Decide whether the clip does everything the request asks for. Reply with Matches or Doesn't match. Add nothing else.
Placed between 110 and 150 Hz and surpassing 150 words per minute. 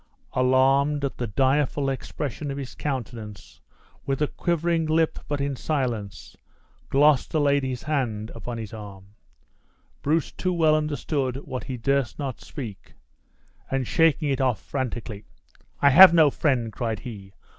Doesn't match